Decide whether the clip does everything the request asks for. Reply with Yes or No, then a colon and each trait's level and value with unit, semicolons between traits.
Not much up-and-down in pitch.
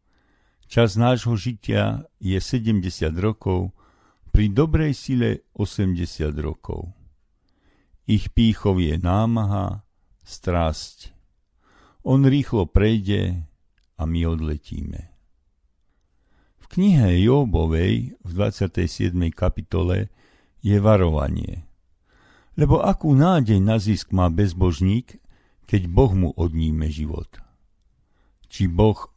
No: average, 4.5 semitones